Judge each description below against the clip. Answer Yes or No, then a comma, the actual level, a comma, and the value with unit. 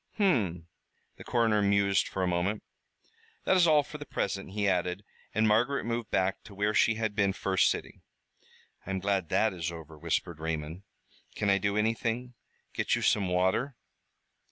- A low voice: Yes, low, 100 Hz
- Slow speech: No, average, 175 wpm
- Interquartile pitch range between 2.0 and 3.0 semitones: No, average, 3.5 semitones